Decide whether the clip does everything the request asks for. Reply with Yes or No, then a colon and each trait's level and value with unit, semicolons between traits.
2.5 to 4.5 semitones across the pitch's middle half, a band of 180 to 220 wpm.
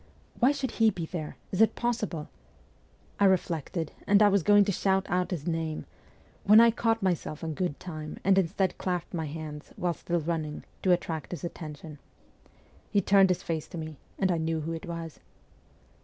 Yes: average, 3.5 semitones; average, 190 wpm